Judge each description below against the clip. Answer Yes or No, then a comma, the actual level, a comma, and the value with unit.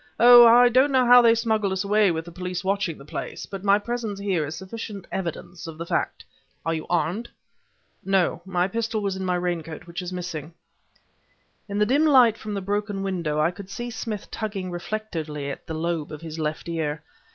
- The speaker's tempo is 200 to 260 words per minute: Yes, fast, 205 wpm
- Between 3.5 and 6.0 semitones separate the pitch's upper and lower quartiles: Yes, average, 4.4 semitones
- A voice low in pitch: No, high, 190 Hz